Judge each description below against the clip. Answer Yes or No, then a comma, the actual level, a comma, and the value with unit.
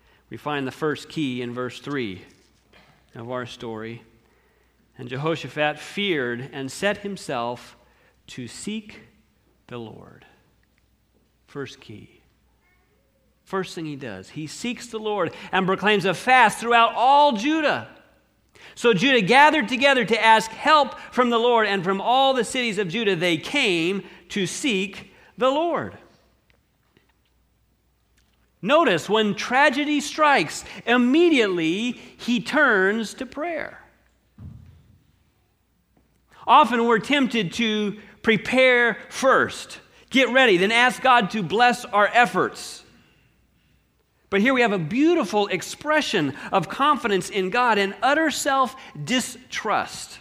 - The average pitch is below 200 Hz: No, high, 215 Hz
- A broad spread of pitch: Yes, wide, 6.2 semitones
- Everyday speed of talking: No, slow, 120 wpm